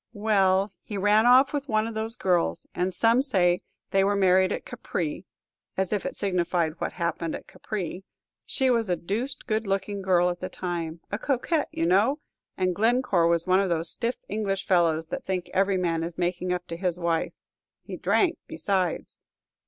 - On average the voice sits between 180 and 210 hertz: Yes, high, 190 Hz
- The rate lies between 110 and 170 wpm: No, average, 185 wpm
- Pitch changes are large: No, average, 3.5 semitones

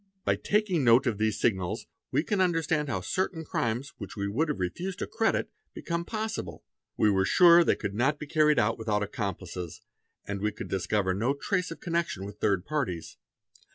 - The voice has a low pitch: Yes, low, 120 Hz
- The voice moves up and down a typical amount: No, wide, 8.7 semitones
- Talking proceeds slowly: No, average, 185 wpm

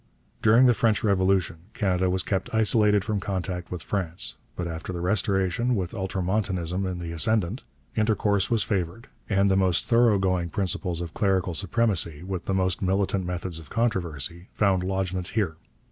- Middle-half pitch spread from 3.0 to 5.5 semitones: No, narrow, 2.6 semitones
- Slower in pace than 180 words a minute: Yes, average, 160 wpm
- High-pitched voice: No, very low, 95 Hz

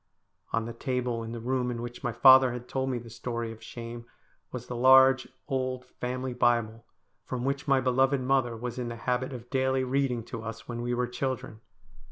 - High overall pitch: No, low, 125 Hz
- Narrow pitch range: Yes, narrow, 1.8 semitones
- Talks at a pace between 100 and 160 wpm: No, fast, 205 wpm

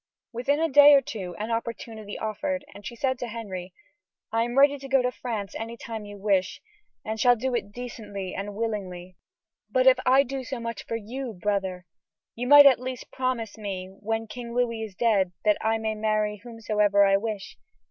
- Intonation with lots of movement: No, average, 3.4 semitones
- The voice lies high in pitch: Yes, high, 225 Hz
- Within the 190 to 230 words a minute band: Yes, average, 195 wpm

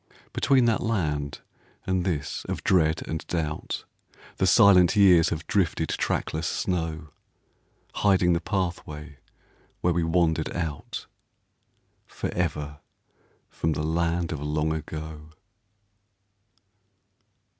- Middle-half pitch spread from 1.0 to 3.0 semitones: Yes, narrow, 2.6 semitones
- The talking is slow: Yes, slow, 100 wpm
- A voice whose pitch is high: No, very low, 80 Hz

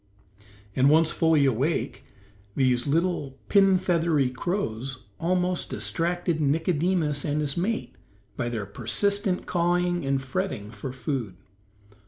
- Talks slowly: Yes, slow, 115 wpm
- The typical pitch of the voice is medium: Yes, medium, 155 Hz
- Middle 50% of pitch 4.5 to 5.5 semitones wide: Yes, average, 5.1 semitones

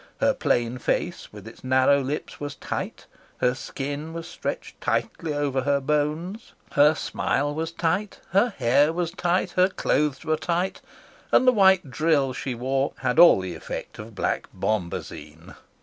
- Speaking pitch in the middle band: Yes, medium, 145 Hz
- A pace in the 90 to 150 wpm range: No, average, 160 wpm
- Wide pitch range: No, average, 4.7 semitones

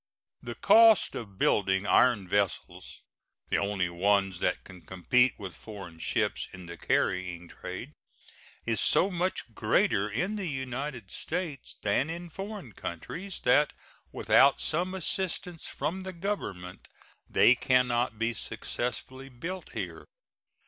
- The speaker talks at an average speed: No, slow, 130 wpm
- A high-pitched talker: No, low, 120 Hz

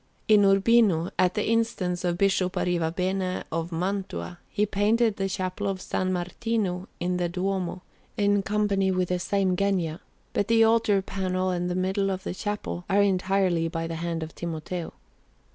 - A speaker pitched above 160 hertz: Yes, medium, 185 Hz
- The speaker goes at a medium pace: Yes, average, 165 wpm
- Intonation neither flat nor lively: No, narrow, 2.1 semitones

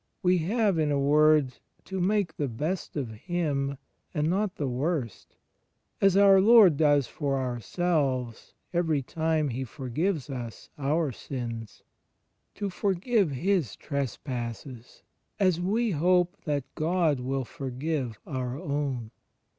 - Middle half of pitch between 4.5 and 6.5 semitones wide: Yes, average, 5.3 semitones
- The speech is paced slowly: Yes, slow, 125 wpm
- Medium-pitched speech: Yes, medium, 150 Hz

